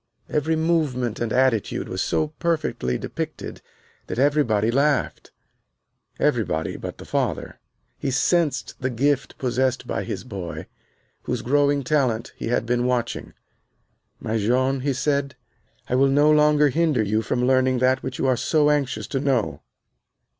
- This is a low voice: Yes, low, 130 Hz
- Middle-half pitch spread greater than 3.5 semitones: No, average, 3.2 semitones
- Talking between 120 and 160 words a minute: Yes, average, 145 wpm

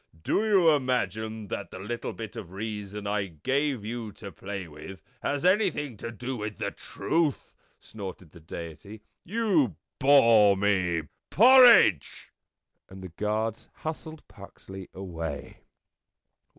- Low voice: Yes, low, 105 Hz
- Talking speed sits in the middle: No, slow, 130 wpm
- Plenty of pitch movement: Yes, wide, 6.3 semitones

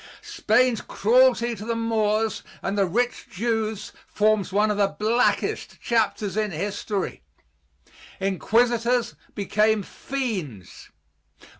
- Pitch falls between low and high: No, high, 215 Hz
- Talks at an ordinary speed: No, slow, 105 wpm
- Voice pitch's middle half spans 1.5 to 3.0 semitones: Yes, narrow, 2.6 semitones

